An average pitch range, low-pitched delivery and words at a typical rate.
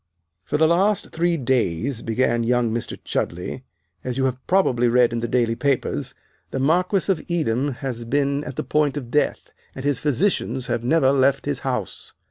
Yes: average, 3.7 semitones; low, 130 Hz; average, 180 wpm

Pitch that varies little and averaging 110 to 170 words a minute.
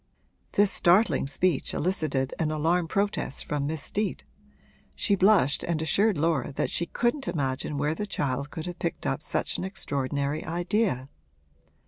No: average, 5.0 semitones; average, 150 wpm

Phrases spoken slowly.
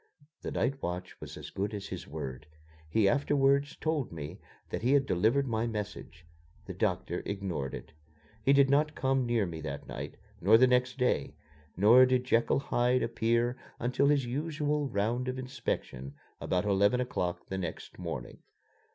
No: average, 165 wpm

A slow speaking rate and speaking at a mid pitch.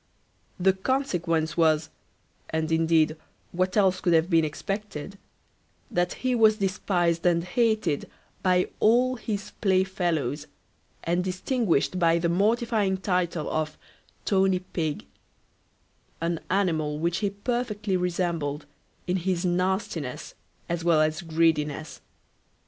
Yes: slow, 115 wpm; medium, 180 Hz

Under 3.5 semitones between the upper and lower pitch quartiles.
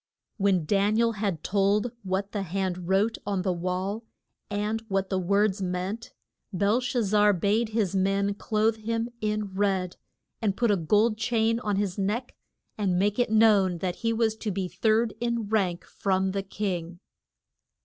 Yes: narrow, 2.5 semitones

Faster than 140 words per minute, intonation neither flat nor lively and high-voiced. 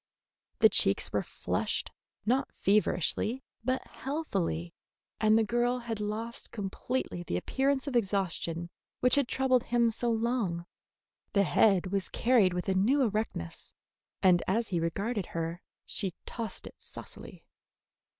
No: slow, 135 wpm; average, 4.8 semitones; high, 215 Hz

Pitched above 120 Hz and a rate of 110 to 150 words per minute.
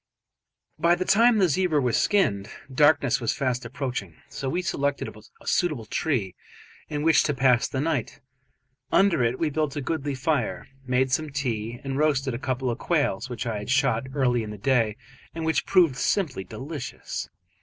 No: low, 135 Hz; average, 175 wpm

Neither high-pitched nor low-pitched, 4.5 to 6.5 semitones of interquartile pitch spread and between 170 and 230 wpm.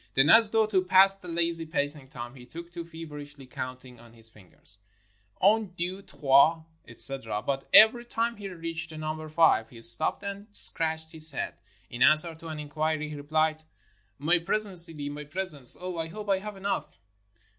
Yes: medium, 160 Hz; average, 4.8 semitones; average, 190 wpm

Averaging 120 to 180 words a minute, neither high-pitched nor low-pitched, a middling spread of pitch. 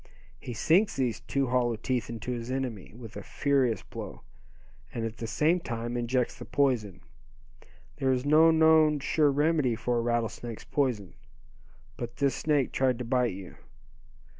No: average, 160 wpm; low, 125 Hz; average, 3.4 semitones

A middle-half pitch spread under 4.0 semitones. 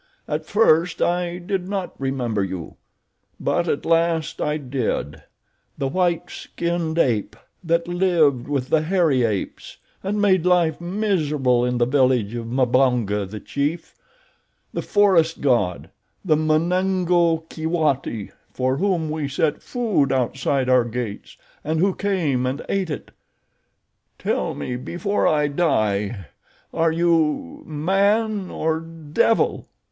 No: wide, 5.5 semitones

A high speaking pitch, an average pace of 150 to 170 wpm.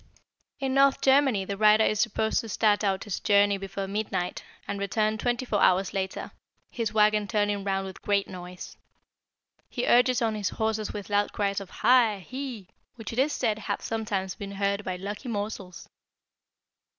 No: high, 205 Hz; average, 185 wpm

